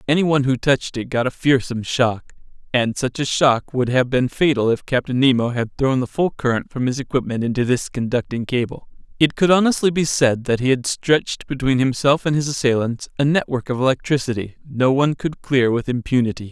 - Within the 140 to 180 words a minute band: No, average, 200 wpm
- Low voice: Yes, low, 130 Hz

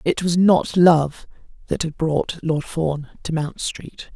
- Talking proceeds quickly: No, average, 175 wpm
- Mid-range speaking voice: Yes, medium, 160 Hz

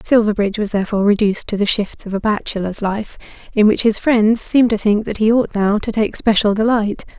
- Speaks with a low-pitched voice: No, high, 215 Hz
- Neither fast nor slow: No, fast, 215 wpm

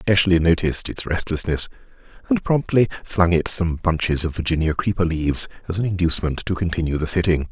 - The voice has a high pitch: No, very low, 85 Hz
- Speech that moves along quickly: No, average, 170 wpm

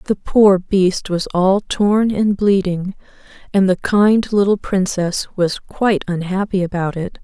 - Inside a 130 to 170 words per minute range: Yes, average, 150 wpm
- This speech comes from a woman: Yes, female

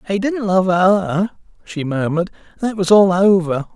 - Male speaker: Yes, male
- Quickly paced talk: No, average, 160 wpm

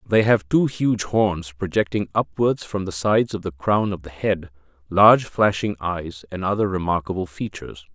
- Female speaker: No, male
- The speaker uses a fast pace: No, average, 175 wpm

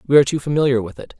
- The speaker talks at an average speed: No, fast, 300 wpm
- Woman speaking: No, male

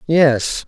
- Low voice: No, medium, 145 Hz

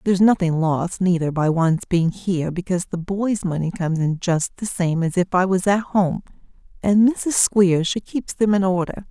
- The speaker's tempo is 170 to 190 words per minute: No, fast, 205 wpm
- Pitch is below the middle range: No, medium, 185 Hz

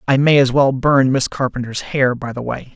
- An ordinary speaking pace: No, fast, 240 wpm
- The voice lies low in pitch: Yes, low, 130 Hz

